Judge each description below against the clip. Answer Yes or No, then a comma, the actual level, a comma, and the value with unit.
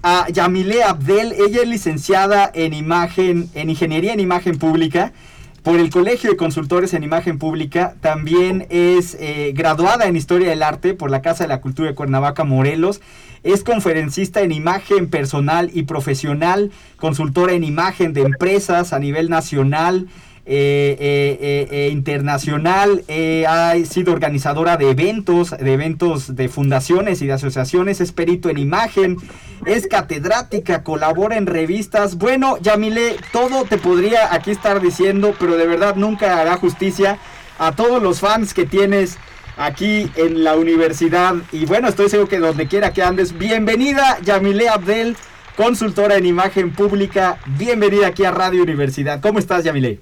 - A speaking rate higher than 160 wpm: No, average, 150 wpm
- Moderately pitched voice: Yes, medium, 175 Hz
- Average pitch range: Yes, average, 4.0 semitones